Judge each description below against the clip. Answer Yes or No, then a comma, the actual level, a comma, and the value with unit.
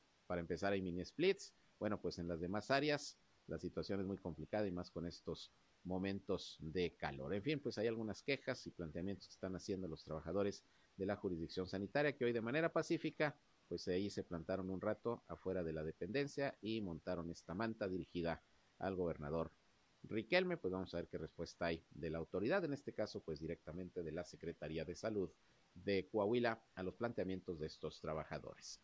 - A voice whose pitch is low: Yes, very low, 95 Hz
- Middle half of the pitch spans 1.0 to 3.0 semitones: No, average, 4.5 semitones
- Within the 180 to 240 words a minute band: Yes, fast, 190 wpm